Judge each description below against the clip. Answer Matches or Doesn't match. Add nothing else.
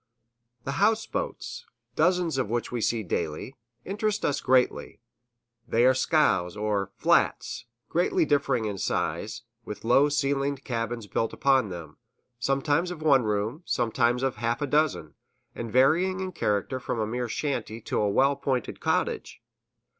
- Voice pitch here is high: Doesn't match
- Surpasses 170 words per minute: Doesn't match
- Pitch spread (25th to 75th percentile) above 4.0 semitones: Matches